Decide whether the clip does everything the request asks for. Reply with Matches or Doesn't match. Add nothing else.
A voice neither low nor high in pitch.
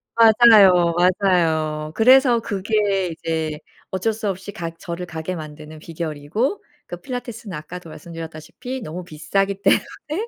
Matches